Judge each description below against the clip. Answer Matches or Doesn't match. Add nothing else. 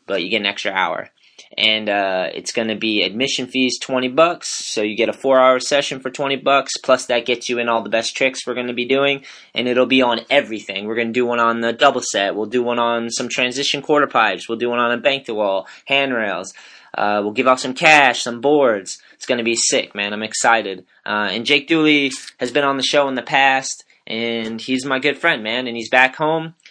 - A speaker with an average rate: Doesn't match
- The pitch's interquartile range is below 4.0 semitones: Matches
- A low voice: Matches